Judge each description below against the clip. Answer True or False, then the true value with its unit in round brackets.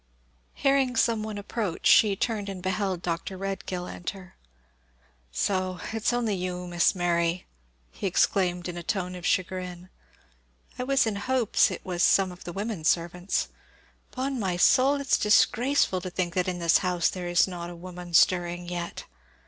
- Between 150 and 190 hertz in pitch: True (185 Hz)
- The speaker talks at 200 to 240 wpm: False (165 wpm)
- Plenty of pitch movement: False (3.0 semitones)